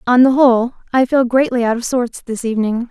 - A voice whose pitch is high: Yes, high, 245 Hz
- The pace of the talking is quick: Yes, fast, 225 wpm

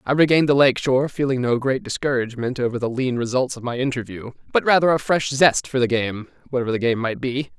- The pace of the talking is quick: Yes, fast, 230 wpm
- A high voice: No, low, 130 Hz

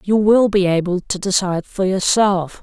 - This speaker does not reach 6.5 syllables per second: Yes, 4.7 syllables/s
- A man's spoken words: Yes, male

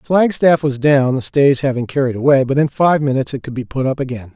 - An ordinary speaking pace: No, fast, 260 wpm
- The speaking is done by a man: Yes, male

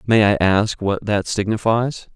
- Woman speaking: No, male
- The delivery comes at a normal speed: Yes, average, 165 wpm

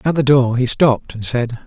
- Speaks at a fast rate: Yes, fast, 250 wpm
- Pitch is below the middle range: Yes, low, 125 Hz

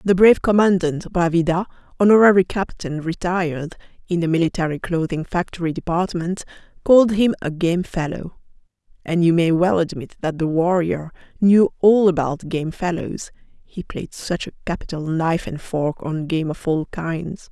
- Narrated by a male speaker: No, female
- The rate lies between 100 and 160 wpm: Yes, average, 145 wpm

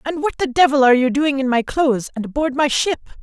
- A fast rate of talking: Yes, fast, 260 wpm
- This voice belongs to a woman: Yes, female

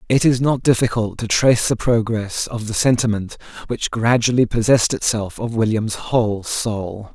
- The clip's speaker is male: Yes, male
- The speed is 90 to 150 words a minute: No, average, 160 wpm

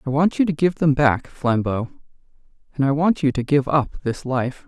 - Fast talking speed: Yes, fast, 220 wpm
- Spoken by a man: Yes, male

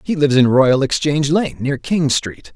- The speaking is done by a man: Yes, male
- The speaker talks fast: Yes, fast, 210 wpm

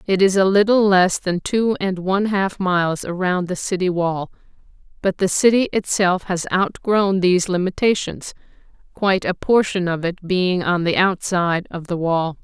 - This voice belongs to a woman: Yes, female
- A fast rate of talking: No, average, 170 wpm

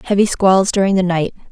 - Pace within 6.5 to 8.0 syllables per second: No, 5.7 syllables/s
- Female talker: Yes, female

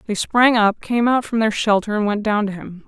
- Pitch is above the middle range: Yes, high, 215 Hz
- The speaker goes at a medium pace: No, fast, 270 wpm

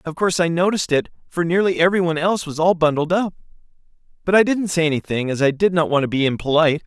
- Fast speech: Yes, fast, 225 wpm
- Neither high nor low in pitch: Yes, medium, 165 Hz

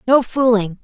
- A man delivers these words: No, female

